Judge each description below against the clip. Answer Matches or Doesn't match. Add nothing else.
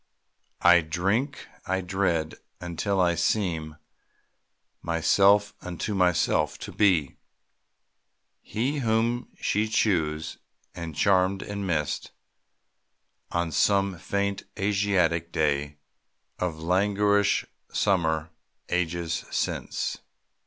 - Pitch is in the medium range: Doesn't match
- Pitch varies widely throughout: Doesn't match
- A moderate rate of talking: Doesn't match